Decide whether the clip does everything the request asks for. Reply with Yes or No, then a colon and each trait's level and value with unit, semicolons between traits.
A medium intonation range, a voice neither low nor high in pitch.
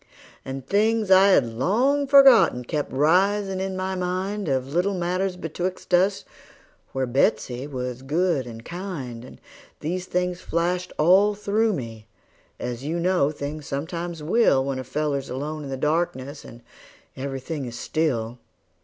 No: wide, 5.9 semitones; medium, 160 Hz